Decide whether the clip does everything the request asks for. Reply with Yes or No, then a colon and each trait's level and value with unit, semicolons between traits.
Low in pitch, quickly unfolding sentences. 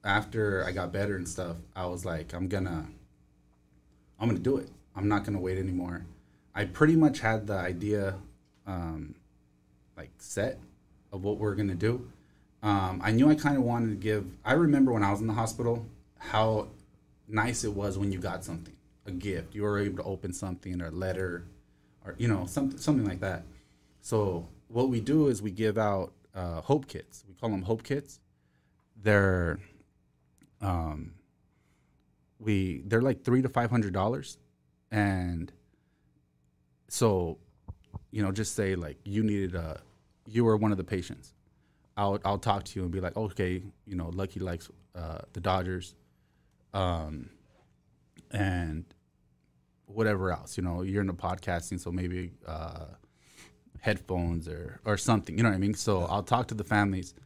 No: very low, 95 Hz; average, 170 wpm